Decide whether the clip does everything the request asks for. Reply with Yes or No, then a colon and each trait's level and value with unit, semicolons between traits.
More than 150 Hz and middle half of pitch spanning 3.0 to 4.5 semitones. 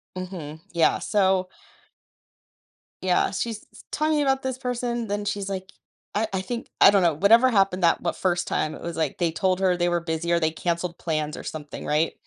Yes: medium, 185 Hz; average, 3.5 semitones